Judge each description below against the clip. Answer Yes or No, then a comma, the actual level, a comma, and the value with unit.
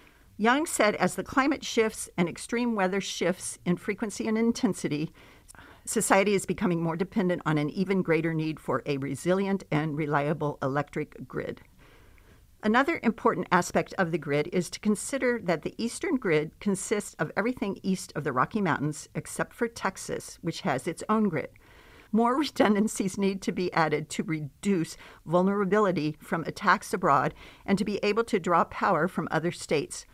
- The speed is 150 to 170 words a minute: Yes, average, 165 wpm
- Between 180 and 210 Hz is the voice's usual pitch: Yes, high, 190 Hz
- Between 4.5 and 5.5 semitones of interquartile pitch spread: Yes, average, 5.2 semitones